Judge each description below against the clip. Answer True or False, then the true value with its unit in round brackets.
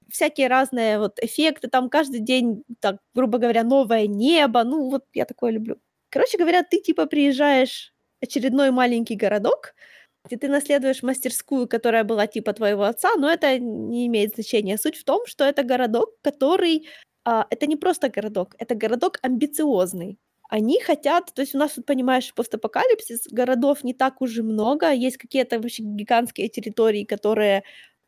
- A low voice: False (255 Hz)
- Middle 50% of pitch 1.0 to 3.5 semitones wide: False (4.0 semitones)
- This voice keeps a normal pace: False (160 wpm)